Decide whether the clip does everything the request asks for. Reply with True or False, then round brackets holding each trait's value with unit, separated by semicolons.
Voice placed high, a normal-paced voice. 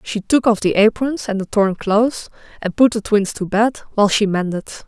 False (210 Hz; 220 wpm)